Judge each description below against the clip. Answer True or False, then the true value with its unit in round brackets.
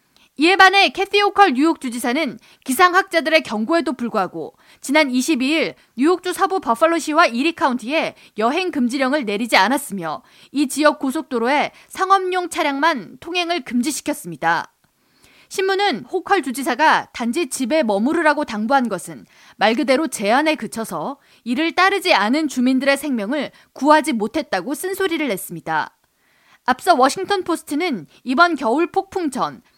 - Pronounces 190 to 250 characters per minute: False (325 characters per minute)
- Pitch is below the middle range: False (300 Hz)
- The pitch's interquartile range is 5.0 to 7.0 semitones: True (5.4 semitones)